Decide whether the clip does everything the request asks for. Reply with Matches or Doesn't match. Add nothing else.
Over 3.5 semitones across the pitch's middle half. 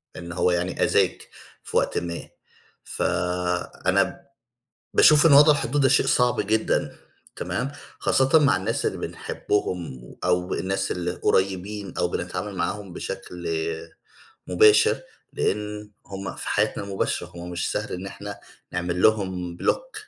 Doesn't match